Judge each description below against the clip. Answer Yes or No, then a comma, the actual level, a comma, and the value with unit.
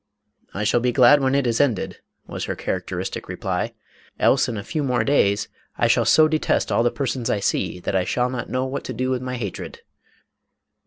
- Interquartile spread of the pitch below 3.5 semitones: Yes, narrow, 2.5 semitones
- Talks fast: Yes, fast, 220 wpm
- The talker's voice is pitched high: No, low, 125 Hz